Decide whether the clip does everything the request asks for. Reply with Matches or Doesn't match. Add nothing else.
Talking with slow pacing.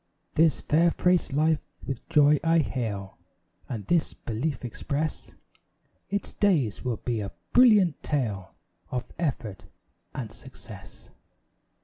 Matches